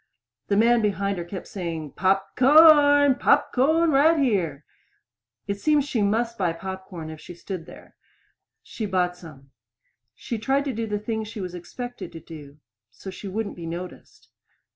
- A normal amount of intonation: No, wide, 5.8 semitones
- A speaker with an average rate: Yes, average, 170 wpm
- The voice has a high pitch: Yes, high, 200 Hz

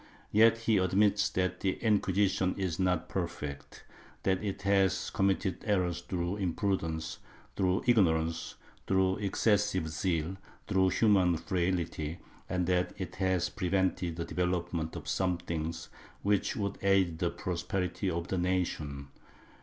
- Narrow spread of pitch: Yes, narrow, 2.3 semitones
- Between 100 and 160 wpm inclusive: Yes, average, 140 wpm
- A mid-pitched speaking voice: No, very low, 90 Hz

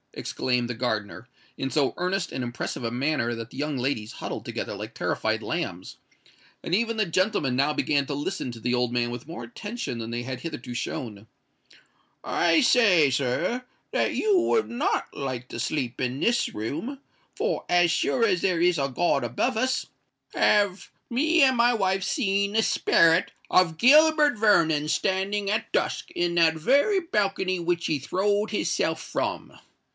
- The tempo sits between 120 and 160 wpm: No, average, 170 wpm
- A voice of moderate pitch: Yes, medium, 170 Hz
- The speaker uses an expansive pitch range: Yes, wide, 8.8 semitones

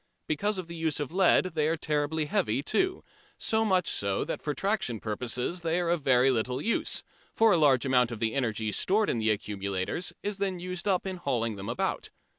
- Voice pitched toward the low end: No, medium, 150 Hz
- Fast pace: Yes, fast, 210 wpm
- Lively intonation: Yes, wide, 7.6 semitones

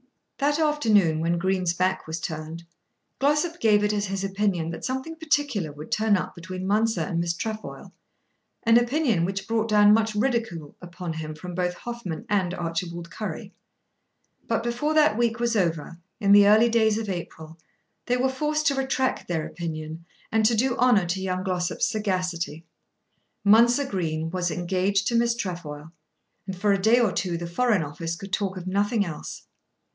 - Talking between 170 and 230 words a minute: Yes, average, 175 wpm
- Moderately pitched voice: No, high, 195 Hz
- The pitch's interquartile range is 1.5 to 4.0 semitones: No, average, 5.1 semitones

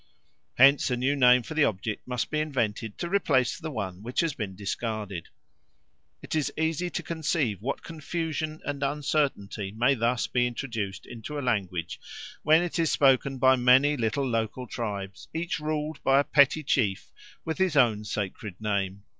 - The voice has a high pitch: No, low, 130 Hz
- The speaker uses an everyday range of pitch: No, wide, 5.7 semitones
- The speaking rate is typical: Yes, average, 170 wpm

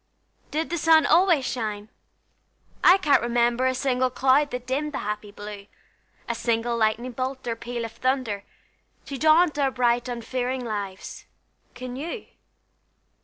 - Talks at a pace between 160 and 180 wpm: No, average, 145 wpm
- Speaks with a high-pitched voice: Yes, very high, 250 Hz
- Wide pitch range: No, average, 3.1 semitones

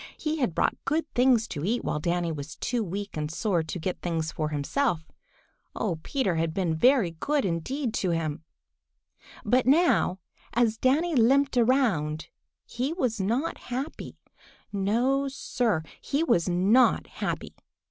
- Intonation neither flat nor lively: No, wide, 7.8 semitones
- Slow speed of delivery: No, average, 145 wpm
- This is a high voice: Yes, high, 220 Hz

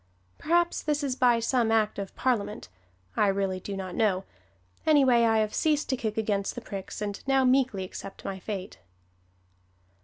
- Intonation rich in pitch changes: No, average, 4.7 semitones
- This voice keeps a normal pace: Yes, average, 165 wpm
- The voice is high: Yes, high, 220 Hz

